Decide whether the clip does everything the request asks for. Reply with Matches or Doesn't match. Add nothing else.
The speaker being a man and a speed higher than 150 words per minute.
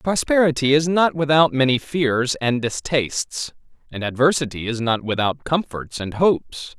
Doesn't match